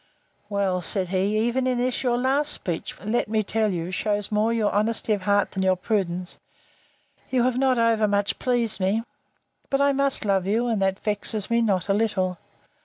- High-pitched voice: Yes, high, 215 Hz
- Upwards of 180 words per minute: Yes, average, 195 wpm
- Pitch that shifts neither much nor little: Yes, average, 3.6 semitones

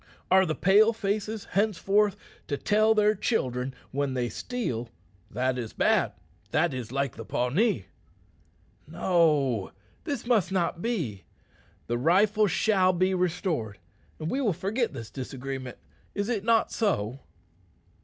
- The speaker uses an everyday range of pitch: No, wide, 8.4 semitones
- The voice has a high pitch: No, medium, 180 Hz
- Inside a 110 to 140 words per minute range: Yes, slow, 135 wpm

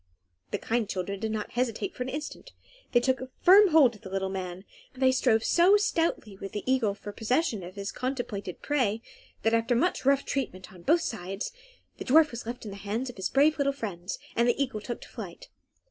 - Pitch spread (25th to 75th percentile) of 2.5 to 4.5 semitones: No, wide, 5.4 semitones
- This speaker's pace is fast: Yes, fast, 215 wpm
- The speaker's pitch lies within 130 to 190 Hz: No, high, 235 Hz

